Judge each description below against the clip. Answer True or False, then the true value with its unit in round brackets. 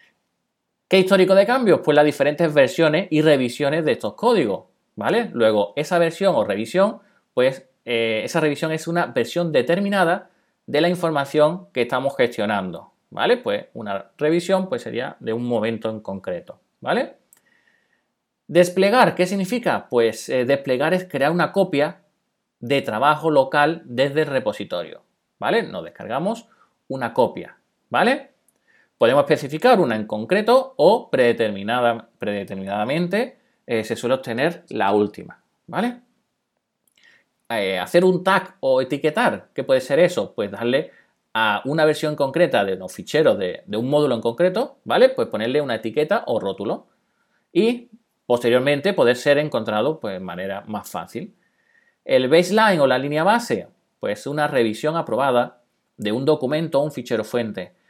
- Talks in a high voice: False (150 Hz)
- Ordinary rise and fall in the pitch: False (6.8 semitones)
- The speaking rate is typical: True (145 wpm)